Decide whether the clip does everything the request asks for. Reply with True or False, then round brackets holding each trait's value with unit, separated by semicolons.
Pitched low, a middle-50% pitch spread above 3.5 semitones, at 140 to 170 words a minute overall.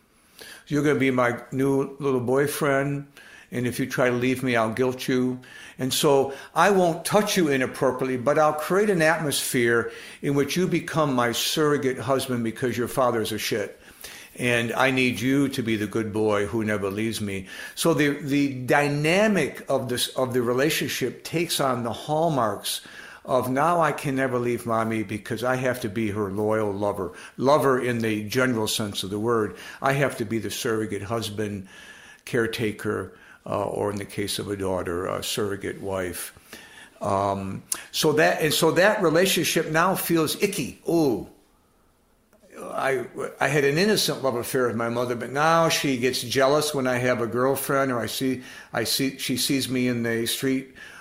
False (130 Hz; 4.0 semitones; 185 wpm)